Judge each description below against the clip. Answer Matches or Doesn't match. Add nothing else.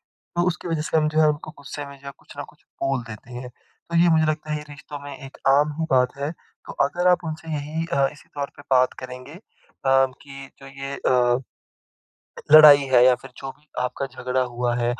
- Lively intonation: Doesn't match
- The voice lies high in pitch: Doesn't match